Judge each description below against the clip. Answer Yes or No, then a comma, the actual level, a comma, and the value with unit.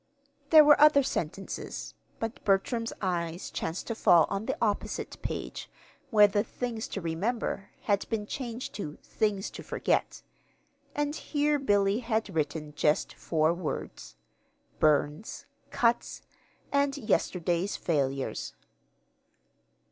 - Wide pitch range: Yes, wide, 6.0 semitones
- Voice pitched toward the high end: Yes, high, 205 Hz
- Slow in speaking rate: Yes, slow, 115 wpm